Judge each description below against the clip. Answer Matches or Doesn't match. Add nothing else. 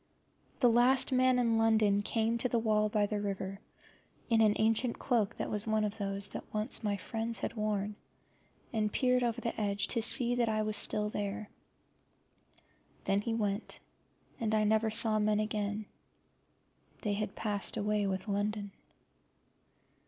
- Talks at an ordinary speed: Matches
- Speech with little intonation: Matches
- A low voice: Doesn't match